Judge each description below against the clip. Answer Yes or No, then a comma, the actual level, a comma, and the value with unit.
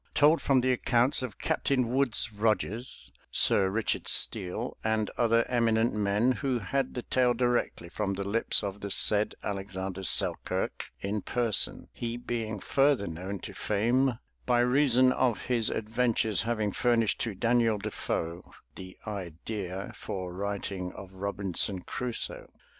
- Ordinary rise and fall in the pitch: Yes, average, 3.6 semitones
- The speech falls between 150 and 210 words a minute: No, average, 140 wpm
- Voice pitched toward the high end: No, low, 110 Hz